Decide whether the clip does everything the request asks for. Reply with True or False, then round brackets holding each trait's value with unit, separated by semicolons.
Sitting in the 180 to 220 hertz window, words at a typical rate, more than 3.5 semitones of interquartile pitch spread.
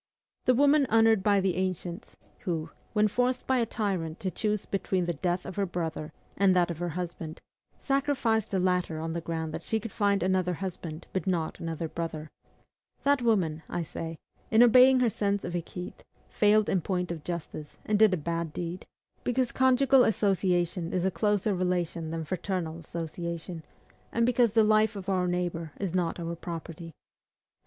True (185 Hz; 180 wpm; 4.1 semitones)